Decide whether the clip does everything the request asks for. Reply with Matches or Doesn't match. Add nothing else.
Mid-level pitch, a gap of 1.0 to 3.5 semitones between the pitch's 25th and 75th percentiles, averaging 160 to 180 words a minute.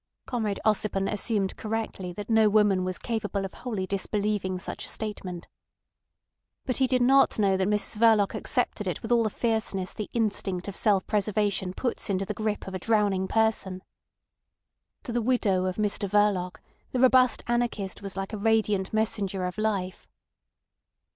Doesn't match